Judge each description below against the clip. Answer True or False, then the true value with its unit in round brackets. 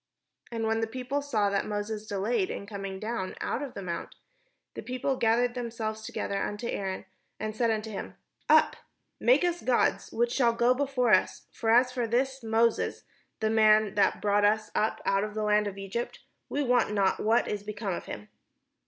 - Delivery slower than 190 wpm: False (195 wpm)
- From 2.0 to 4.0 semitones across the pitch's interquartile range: True (2.7 semitones)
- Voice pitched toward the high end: True (220 Hz)